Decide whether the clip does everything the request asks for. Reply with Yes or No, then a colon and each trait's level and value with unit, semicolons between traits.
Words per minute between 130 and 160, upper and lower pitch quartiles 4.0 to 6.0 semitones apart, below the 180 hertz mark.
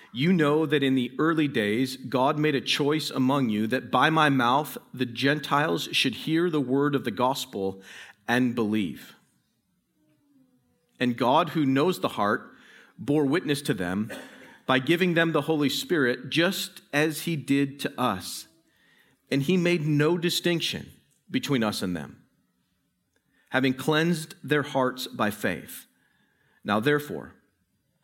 No: average, 145 wpm; average, 3.5 semitones; medium, 140 Hz